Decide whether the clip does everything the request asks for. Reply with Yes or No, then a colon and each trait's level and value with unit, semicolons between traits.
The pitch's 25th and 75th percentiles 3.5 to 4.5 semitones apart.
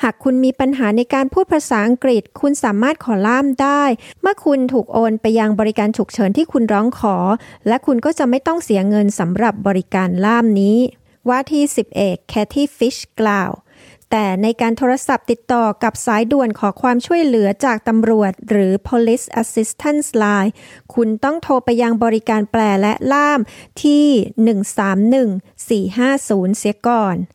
Yes: average, 3.9 semitones